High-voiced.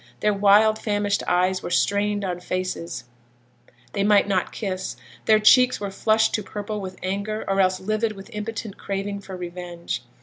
Yes: high, 200 Hz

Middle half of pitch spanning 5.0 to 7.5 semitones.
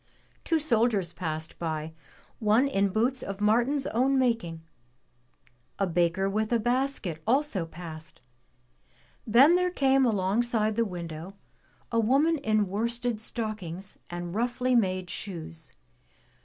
Yes: wide, 5.5 semitones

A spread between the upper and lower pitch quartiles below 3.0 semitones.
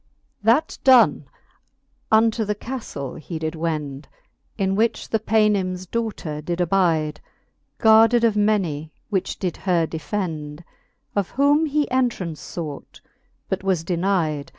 No: wide, 5.5 semitones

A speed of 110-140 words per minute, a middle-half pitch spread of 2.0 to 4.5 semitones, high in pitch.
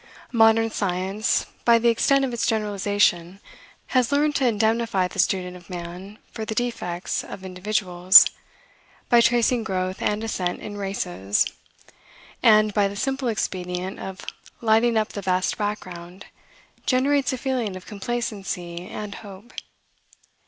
Yes: slow, 135 wpm; average, 3.8 semitones; high, 205 Hz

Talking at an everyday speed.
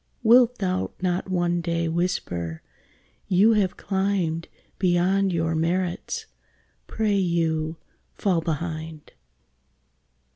No: slow, 95 wpm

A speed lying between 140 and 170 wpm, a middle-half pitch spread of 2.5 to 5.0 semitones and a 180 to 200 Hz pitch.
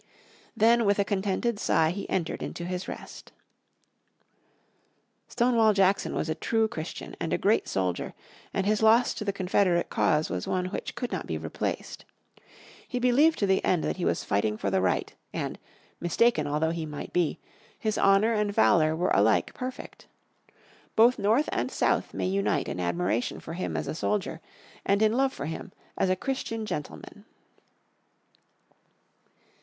No: average, 165 wpm; wide, 5.6 semitones; high, 190 Hz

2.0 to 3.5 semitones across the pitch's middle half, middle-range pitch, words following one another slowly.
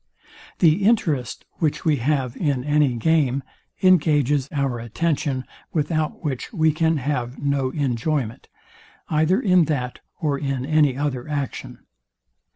Yes: average, 3.1 semitones; medium, 145 Hz; slow, 125 wpm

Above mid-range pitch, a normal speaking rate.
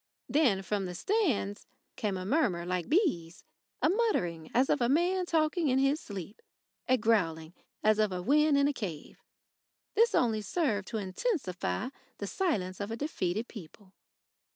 Yes: high, 220 Hz; average, 155 wpm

